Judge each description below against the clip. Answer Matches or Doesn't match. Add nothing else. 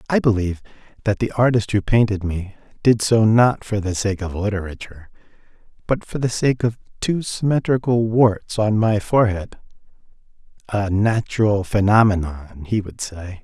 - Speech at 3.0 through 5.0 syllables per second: Matches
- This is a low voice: Matches